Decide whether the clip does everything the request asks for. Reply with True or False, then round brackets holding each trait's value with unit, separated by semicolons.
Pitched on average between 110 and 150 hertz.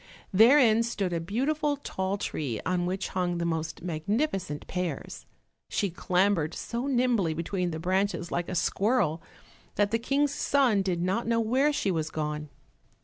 False (190 Hz)